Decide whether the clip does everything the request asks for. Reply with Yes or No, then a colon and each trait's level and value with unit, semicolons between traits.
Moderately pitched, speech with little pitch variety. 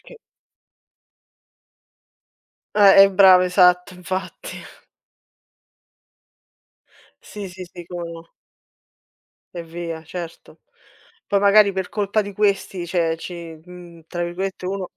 Yes: medium, 180 Hz; narrow, 2.3 semitones